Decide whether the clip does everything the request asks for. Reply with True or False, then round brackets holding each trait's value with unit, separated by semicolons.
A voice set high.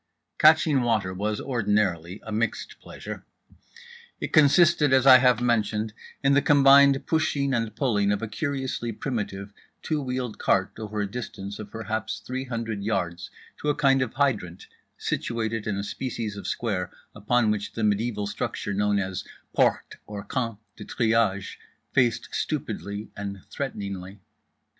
False (110 Hz)